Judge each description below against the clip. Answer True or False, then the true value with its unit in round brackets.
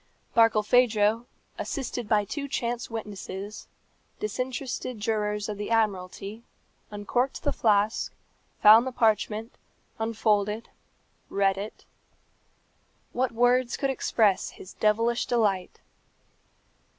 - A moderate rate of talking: False (95 wpm)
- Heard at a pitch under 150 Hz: False (220 Hz)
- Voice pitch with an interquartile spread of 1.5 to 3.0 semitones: True (2.6 semitones)